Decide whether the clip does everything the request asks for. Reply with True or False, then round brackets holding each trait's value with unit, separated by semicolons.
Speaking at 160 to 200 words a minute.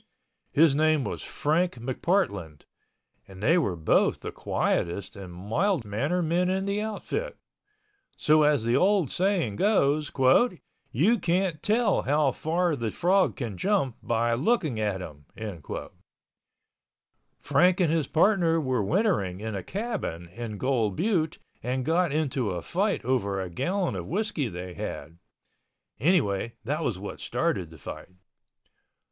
False (135 wpm)